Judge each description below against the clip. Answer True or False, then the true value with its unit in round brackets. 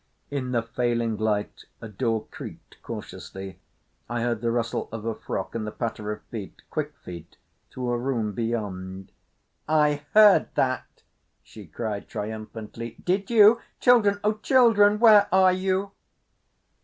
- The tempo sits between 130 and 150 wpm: True (140 wpm)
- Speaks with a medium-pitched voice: False (120 Hz)